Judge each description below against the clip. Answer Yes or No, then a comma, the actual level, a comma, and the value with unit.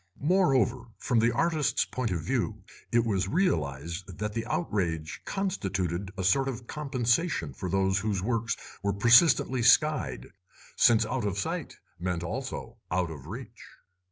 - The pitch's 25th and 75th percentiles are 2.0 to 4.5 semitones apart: No, wide, 5.5 semitones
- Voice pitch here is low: Yes, low, 110 Hz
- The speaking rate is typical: Yes, average, 145 wpm